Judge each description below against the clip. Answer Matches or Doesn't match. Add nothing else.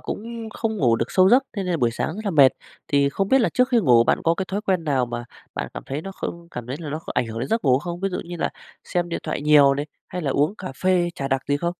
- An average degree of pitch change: Doesn't match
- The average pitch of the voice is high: Doesn't match